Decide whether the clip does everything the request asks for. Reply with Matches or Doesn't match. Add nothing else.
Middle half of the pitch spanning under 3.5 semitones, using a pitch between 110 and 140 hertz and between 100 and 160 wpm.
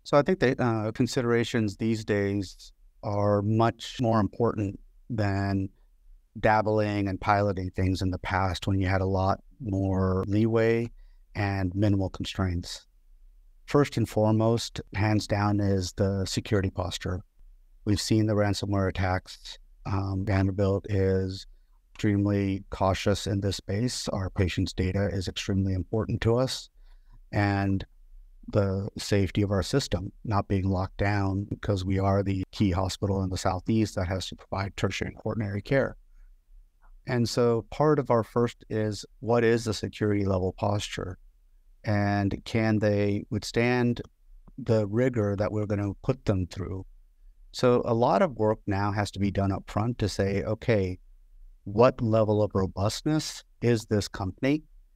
Doesn't match